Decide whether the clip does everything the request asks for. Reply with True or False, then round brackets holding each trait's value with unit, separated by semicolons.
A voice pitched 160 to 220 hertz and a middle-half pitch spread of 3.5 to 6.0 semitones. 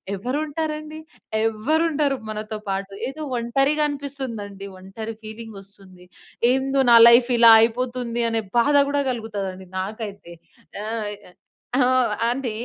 False (230 Hz; 4.7 semitones)